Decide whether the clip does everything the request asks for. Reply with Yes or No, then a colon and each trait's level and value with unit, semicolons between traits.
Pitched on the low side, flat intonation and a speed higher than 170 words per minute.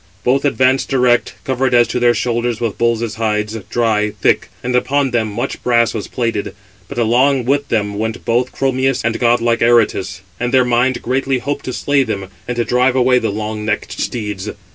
Yes: low, 120 Hz; narrow, 2.3 semitones; average, 190 wpm